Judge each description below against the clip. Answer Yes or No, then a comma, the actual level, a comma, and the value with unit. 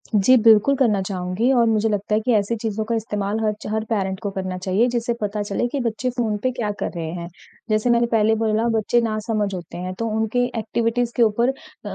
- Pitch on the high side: Yes, high, 215 Hz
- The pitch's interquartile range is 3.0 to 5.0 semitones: No, narrow, 2.5 semitones